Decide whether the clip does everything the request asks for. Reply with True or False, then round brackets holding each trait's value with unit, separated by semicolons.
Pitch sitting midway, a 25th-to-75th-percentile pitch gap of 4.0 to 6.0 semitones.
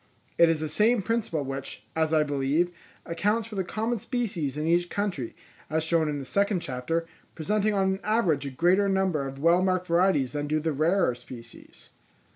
True (165 Hz; 4.8 semitones)